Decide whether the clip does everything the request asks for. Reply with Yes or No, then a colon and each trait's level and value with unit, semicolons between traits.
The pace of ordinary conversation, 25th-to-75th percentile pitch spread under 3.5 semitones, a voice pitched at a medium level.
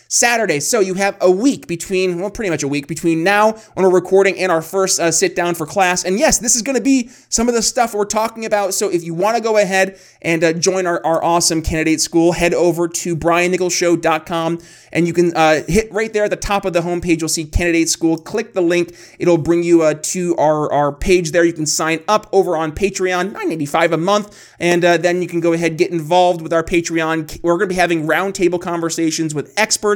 No: fast, 235 wpm; average, 2.8 semitones; medium, 175 Hz